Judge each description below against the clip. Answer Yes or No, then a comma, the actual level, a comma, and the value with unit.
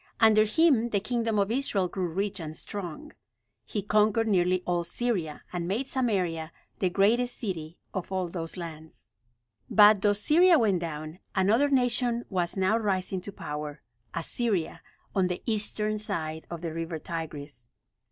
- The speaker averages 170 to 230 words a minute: No, average, 150 wpm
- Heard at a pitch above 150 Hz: Yes, high, 190 Hz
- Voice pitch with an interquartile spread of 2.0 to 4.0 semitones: No, average, 4.6 semitones